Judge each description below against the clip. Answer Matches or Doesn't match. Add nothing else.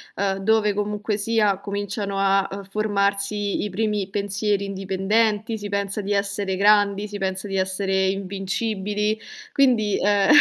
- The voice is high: Matches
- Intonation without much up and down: Matches